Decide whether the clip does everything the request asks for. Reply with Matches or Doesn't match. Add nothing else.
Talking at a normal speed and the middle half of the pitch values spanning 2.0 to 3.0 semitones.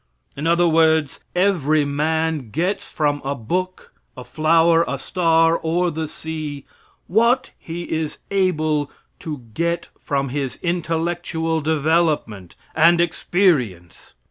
Doesn't match